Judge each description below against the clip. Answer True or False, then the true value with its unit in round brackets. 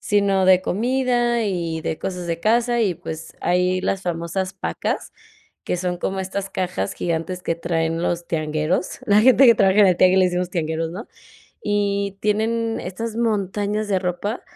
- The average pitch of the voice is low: False (190 Hz)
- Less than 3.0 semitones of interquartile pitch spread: False (3.3 semitones)